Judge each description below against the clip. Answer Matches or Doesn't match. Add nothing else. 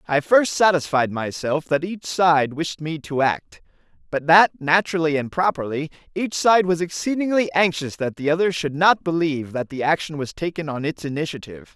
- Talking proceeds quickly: Doesn't match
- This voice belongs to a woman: Doesn't match